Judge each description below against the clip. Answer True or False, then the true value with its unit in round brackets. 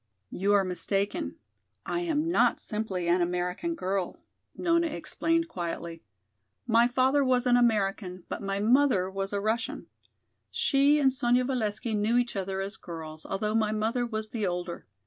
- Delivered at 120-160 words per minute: True (155 wpm)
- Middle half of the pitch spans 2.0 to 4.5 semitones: False (4.9 semitones)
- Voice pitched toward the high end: True (215 Hz)